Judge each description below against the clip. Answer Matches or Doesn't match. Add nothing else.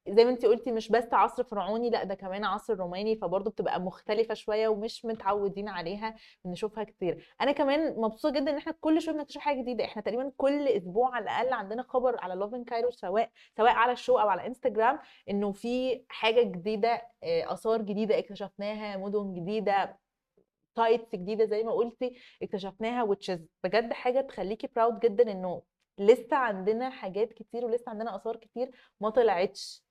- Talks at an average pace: Doesn't match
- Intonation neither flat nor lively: Matches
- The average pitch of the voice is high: Matches